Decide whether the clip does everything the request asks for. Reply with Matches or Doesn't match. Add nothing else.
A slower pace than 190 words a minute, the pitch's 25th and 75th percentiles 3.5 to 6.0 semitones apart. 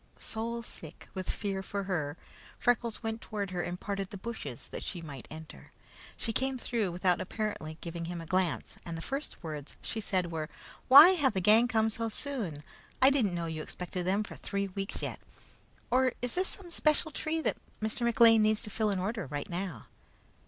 Doesn't match